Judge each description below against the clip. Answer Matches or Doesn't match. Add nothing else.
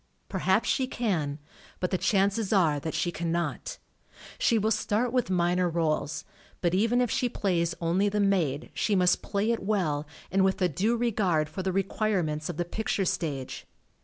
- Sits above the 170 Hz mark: Matches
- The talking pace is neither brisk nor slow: Matches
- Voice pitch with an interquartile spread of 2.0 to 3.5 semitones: Doesn't match